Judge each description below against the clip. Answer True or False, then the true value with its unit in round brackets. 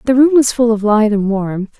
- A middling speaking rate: False (265 wpm)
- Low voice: False (225 Hz)